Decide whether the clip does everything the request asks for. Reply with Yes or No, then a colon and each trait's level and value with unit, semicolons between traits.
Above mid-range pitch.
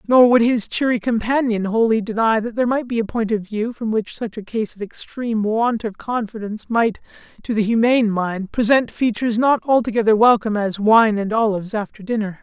Yes: high, 220 Hz